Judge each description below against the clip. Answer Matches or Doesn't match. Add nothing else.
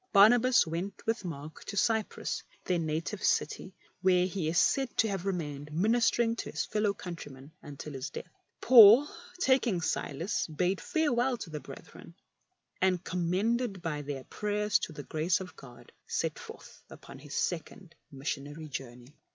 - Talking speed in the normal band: Matches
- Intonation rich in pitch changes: Matches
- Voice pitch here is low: Doesn't match